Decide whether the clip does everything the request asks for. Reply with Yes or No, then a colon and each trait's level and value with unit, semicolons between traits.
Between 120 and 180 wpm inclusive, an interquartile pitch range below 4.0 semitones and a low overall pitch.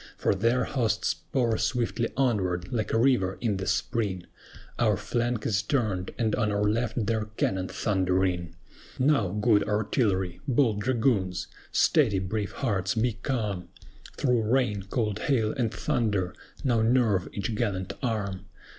Yes: average, 140 wpm; average, 3.6 semitones; low, 110 Hz